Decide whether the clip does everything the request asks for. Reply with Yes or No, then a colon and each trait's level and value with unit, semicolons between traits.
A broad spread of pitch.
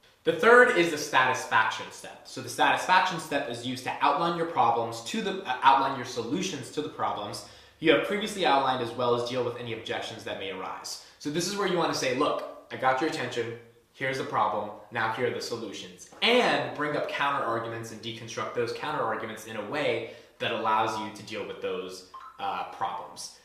Yes: wide, 8.6 semitones